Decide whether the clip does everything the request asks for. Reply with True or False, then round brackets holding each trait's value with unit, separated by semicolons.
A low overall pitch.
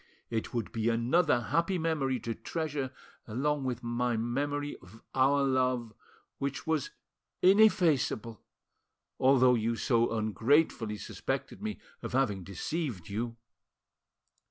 True (130 Hz)